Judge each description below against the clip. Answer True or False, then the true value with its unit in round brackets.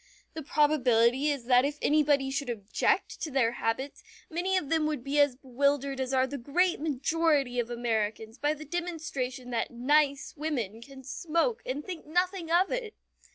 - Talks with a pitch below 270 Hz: False (280 Hz)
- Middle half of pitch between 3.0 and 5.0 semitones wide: True (3.9 semitones)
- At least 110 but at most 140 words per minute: False (170 wpm)